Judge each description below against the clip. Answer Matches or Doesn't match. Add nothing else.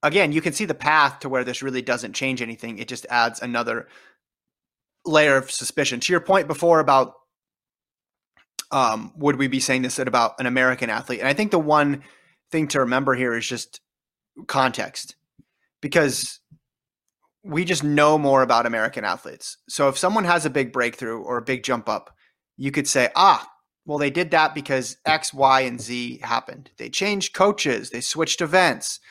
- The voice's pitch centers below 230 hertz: Matches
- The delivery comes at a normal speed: Matches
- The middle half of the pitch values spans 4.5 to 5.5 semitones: Doesn't match